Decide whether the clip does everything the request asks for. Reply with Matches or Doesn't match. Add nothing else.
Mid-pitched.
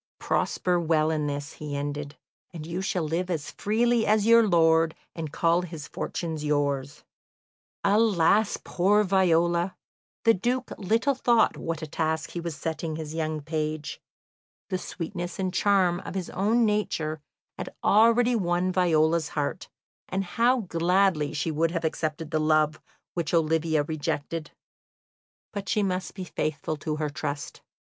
Matches